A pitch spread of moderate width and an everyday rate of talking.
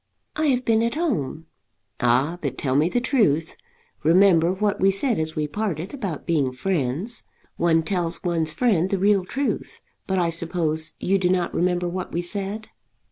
Yes: average, 4.1 semitones; average, 175 wpm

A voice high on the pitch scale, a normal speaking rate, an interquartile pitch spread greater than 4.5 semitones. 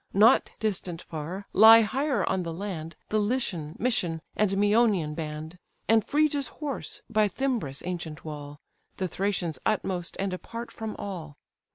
Yes: high, 195 Hz; average, 145 wpm; average, 5.2 semitones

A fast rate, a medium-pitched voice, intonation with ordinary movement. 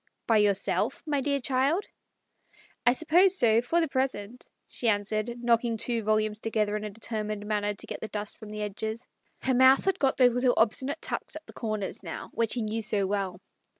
No: fast, 215 wpm; high, 225 Hz; average, 3.6 semitones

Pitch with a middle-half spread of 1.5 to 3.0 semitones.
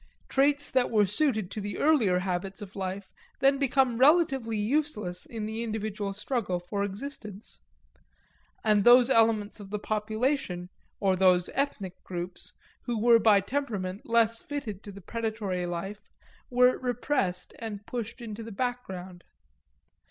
No: average, 4.1 semitones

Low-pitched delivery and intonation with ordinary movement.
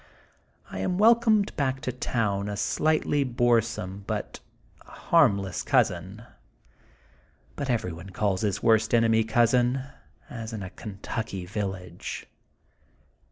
Yes: low, 110 Hz; average, 4.4 semitones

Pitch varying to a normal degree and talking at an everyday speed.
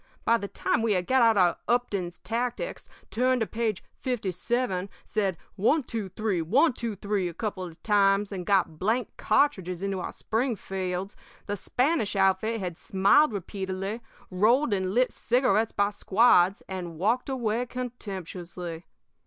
Yes: average, 4.0 semitones; average, 155 wpm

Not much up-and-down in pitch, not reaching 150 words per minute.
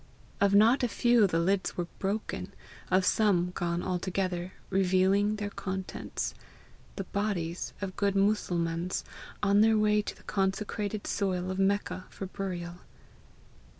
Yes: narrow, 2.1 semitones; slow, 135 wpm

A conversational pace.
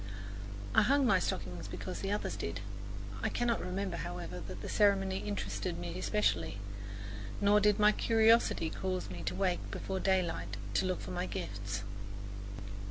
Yes: average, 155 wpm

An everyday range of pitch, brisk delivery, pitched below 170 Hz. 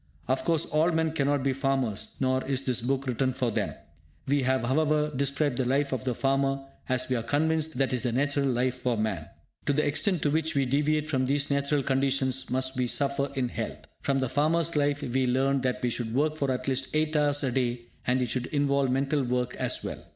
No: narrow, 2.2 semitones; fast, 225 wpm; low, 135 Hz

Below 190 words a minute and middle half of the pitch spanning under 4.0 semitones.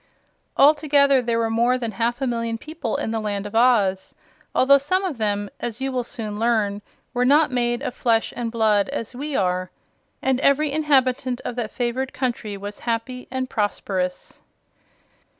Yes: average, 170 wpm; average, 3.3 semitones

